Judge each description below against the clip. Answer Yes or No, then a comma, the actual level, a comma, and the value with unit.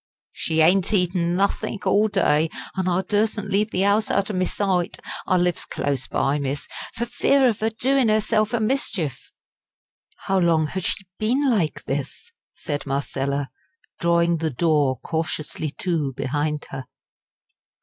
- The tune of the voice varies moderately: No, wide, 5.7 semitones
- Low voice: No, medium, 180 Hz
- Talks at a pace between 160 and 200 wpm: No, average, 150 wpm